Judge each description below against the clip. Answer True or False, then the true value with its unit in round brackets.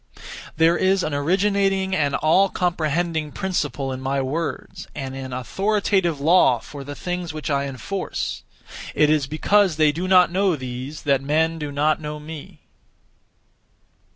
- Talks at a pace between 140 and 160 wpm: True (150 wpm)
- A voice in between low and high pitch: True (155 Hz)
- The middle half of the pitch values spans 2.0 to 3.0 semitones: False (4.3 semitones)